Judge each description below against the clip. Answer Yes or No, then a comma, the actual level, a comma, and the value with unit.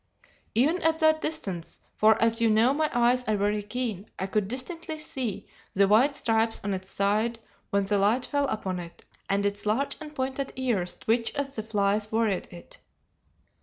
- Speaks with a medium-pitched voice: No, high, 225 Hz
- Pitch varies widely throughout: No, average, 4.6 semitones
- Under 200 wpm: Yes, average, 180 wpm